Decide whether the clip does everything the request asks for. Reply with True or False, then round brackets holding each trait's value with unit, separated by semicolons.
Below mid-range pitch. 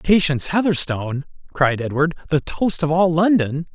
False (160 Hz)